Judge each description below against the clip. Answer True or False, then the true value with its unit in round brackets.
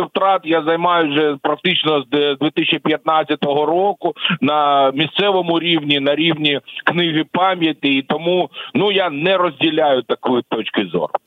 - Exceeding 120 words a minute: True (130 wpm)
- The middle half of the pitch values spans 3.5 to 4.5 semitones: False (2.8 semitones)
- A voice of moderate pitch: True (160 Hz)